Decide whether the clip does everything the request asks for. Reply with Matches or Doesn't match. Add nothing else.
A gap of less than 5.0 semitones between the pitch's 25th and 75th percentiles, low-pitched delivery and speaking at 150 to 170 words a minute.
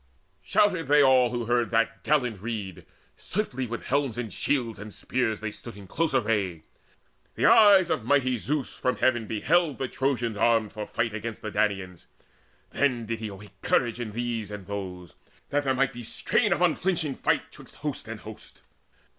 Doesn't match